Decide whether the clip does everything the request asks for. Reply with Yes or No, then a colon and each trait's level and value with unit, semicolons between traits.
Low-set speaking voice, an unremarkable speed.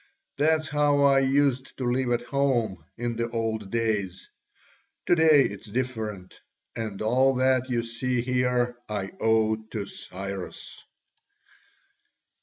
No: low, 120 Hz; slow, 125 wpm